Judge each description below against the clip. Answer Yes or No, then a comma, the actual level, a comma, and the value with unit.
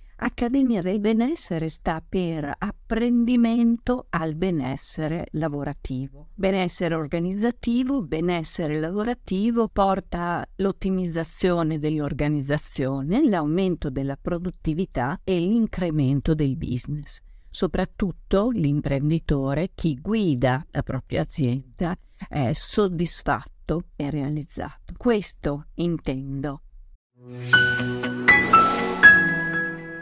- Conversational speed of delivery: No, slow, 70 wpm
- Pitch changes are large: No, average, 5.0 semitones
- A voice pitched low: No, medium, 165 Hz